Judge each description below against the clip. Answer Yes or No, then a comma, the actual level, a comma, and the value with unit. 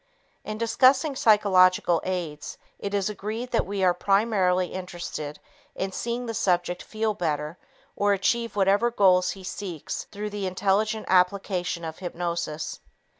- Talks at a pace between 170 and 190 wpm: No, average, 140 wpm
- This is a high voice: Yes, high, 195 Hz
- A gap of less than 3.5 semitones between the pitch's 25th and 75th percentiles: Yes, average, 3.0 semitones